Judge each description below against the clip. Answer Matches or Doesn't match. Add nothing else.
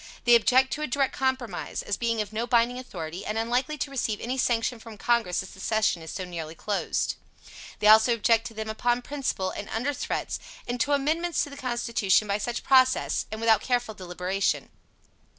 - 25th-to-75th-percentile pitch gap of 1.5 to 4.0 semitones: Matches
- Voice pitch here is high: Matches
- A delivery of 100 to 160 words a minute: Doesn't match